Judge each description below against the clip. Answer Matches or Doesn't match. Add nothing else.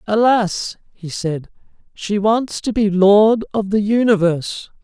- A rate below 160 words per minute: Matches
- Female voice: Doesn't match